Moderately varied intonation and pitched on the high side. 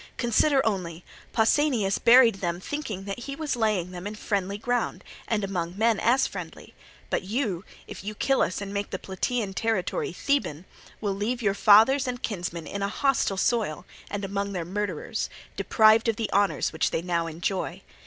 Yes: average, 3.8 semitones; high, 205 Hz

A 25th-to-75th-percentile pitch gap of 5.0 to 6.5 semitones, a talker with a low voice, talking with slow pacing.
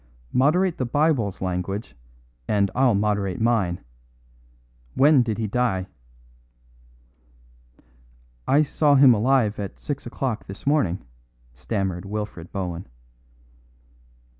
Yes: wide, 5.6 semitones; low, 110 Hz; slow, 100 wpm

